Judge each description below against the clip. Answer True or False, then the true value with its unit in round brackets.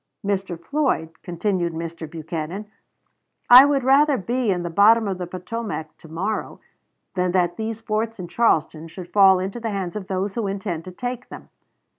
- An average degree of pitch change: True (4.5 semitones)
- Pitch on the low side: False (195 Hz)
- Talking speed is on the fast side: False (175 wpm)